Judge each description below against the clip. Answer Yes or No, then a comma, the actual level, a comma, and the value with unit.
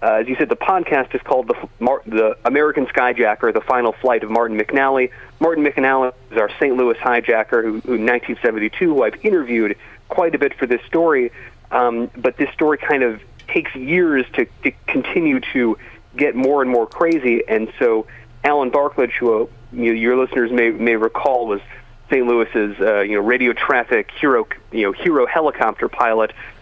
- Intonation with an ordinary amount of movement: Yes, average, 3.1 semitones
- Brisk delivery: No, average, 185 wpm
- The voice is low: Yes, low, 120 Hz